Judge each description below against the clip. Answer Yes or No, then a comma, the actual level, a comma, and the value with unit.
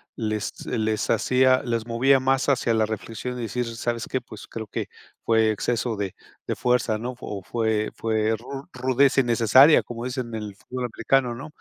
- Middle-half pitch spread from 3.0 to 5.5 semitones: No, narrow, 2.6 semitones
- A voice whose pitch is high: No, low, 115 Hz